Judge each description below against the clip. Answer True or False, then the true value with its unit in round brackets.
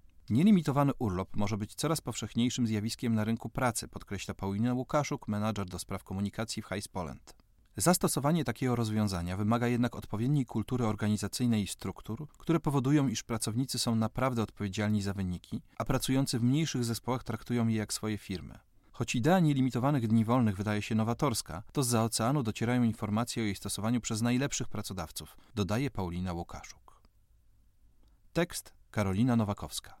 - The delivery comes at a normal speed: True (145 wpm)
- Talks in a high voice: False (115 Hz)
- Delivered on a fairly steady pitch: False (3.4 semitones)